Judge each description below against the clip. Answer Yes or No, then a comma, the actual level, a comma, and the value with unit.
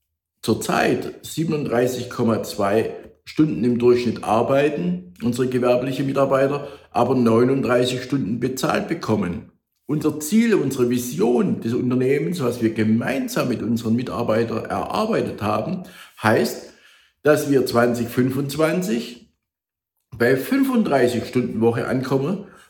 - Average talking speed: No, slow, 100 wpm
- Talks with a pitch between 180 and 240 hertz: No, low, 125 Hz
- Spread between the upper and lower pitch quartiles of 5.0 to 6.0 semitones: No, average, 3.2 semitones